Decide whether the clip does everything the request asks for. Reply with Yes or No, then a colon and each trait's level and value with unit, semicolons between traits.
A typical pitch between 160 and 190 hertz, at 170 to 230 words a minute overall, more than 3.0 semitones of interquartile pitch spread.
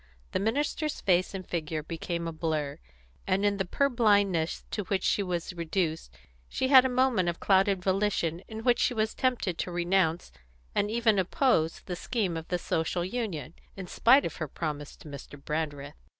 Yes: medium, 185 Hz; average, 180 wpm; average, 4.9 semitones